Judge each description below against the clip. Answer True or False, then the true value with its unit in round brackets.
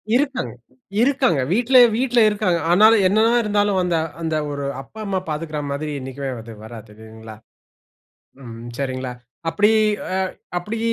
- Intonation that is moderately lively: False (8.3 semitones)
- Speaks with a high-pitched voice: False (175 Hz)